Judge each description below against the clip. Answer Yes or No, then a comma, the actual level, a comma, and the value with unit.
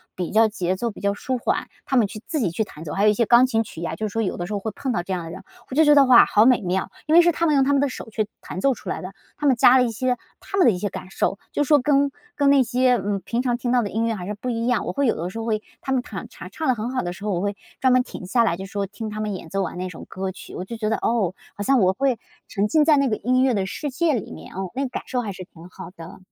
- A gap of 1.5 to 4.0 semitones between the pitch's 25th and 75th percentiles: No, average, 4.9 semitones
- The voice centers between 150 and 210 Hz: No, high, 225 Hz